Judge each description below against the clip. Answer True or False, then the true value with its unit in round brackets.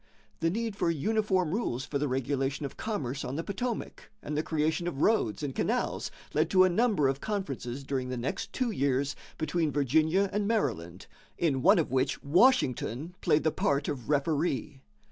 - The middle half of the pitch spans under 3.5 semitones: False (5.6 semitones)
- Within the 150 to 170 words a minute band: False (180 wpm)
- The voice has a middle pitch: True (150 Hz)